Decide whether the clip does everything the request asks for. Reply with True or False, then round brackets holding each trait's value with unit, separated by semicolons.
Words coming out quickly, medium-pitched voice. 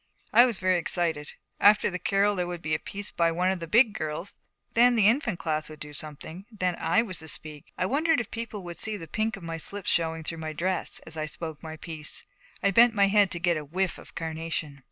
True (240 wpm; 175 Hz)